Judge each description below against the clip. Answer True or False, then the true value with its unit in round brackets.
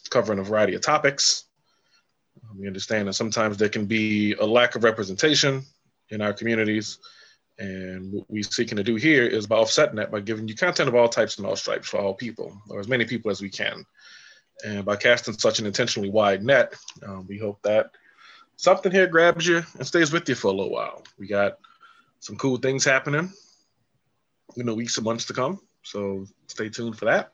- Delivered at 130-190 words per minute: False (200 wpm)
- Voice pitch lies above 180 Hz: False (115 Hz)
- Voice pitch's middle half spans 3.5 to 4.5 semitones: True (4.1 semitones)